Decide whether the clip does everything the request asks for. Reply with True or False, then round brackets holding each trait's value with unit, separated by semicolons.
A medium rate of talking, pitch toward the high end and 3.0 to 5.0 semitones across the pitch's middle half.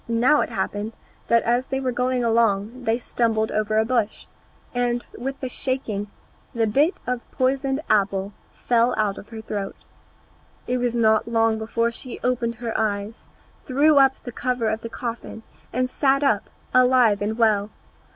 False (165 wpm; 235 Hz; 2.5 semitones)